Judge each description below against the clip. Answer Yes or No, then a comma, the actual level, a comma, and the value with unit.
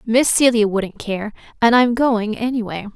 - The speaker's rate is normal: Yes, average, 185 wpm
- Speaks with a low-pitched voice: No, high, 225 Hz